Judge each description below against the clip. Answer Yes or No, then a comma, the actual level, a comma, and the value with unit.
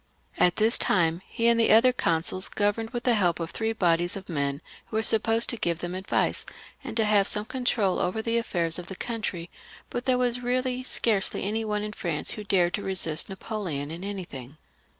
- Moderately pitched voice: No, high, 205 Hz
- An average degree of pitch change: Yes, average, 4.7 semitones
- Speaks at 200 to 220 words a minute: Yes, fast, 205 wpm